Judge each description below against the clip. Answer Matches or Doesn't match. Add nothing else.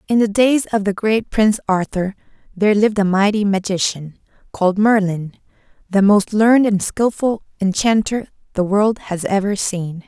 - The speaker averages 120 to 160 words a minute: Matches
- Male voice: Doesn't match